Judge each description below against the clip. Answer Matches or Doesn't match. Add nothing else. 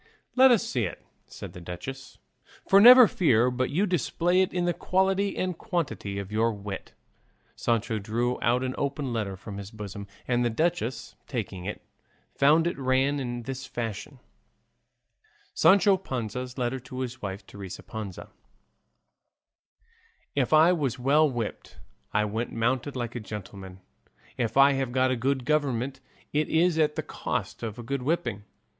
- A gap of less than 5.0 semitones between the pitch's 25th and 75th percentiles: Doesn't match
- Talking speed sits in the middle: Matches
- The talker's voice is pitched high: Doesn't match